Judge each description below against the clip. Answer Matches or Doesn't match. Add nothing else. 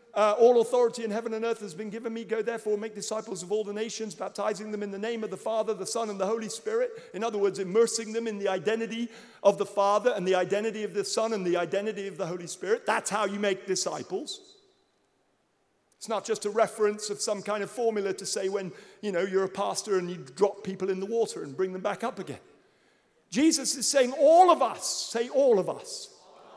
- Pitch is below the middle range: Doesn't match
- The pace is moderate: Doesn't match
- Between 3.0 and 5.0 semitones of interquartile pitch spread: Doesn't match